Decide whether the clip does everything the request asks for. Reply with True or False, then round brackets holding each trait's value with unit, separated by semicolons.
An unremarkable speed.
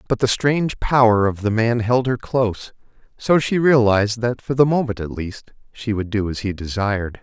False (210 wpm)